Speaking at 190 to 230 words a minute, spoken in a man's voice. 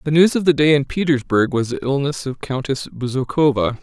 Yes: fast, 205 wpm; male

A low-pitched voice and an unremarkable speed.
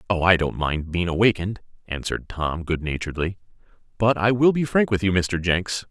Yes: very low, 95 Hz; average, 195 wpm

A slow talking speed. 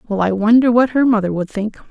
No: fast, 250 wpm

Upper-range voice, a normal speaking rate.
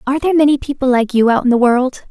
No: very high, 260 Hz; fast, 285 wpm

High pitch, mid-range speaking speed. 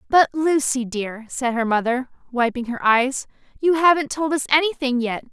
Yes: very high, 265 Hz; average, 170 wpm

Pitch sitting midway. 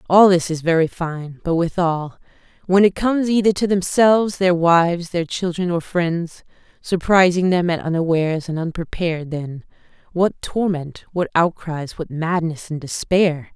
Yes: medium, 170 Hz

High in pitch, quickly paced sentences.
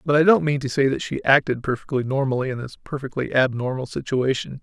No: low, 135 Hz; fast, 210 wpm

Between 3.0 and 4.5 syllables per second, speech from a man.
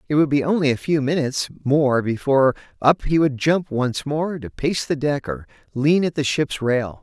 No: 4.9 syllables/s; male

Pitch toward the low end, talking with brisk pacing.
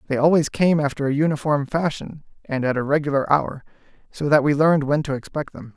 No: medium, 145 Hz; fast, 210 wpm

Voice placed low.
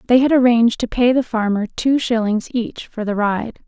No: high, 230 Hz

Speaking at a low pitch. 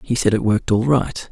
Yes: low, 115 Hz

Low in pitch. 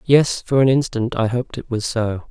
Yes: low, 120 Hz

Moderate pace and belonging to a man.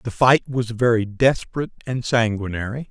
Yes: average, 145 wpm; male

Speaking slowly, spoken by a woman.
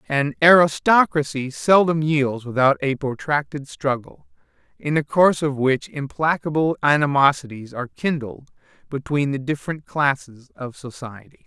No: slow, 120 wpm; male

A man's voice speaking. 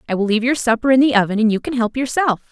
No: female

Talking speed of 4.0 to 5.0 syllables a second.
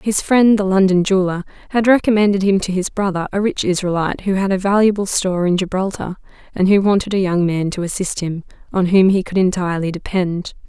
No: 6.0 syllables/s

